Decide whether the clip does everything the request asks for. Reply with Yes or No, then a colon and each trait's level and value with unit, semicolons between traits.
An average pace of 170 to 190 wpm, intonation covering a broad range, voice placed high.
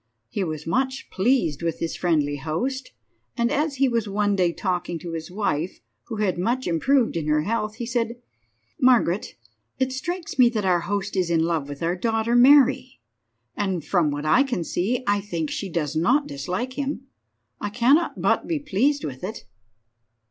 Yes: average, 180 wpm; wide, 7.1 semitones; high, 205 Hz